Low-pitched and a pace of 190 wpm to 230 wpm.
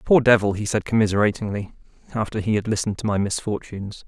No: low, 105 Hz; average, 175 wpm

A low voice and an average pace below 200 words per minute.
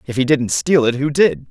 No: low, 130 Hz; fast, 320 wpm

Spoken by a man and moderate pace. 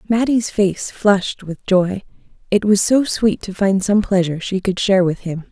No: female; average, 195 wpm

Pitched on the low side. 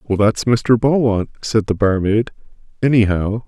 Yes: low, 110 Hz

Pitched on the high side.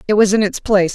Yes: high, 205 Hz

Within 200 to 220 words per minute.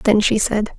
No: fast, 230 wpm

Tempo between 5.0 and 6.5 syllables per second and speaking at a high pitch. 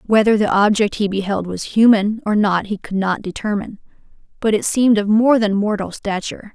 Yes: 5.5 syllables/s; high, 210 Hz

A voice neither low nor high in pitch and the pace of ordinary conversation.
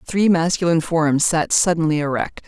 Yes: medium, 165 Hz; average, 145 wpm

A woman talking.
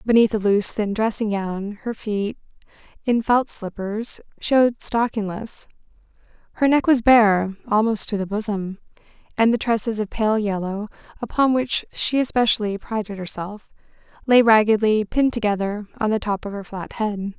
Yes: female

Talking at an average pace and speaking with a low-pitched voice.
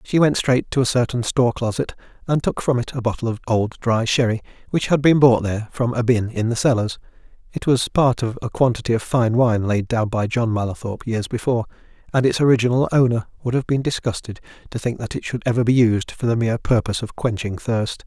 No: fast, 220 wpm; low, 120 Hz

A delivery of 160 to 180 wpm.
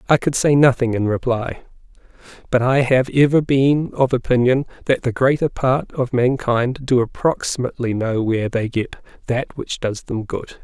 Yes: average, 170 wpm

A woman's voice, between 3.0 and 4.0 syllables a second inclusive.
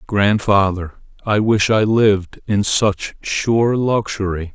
No: male; 3.5 syllables/s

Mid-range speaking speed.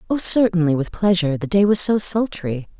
Yes: average, 195 wpm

